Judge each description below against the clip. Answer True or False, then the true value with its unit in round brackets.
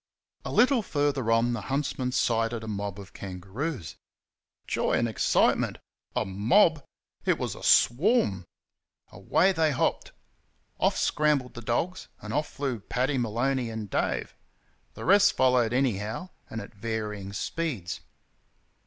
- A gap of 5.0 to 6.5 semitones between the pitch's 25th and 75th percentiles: True (5.4 semitones)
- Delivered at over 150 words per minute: False (135 wpm)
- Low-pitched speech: True (120 Hz)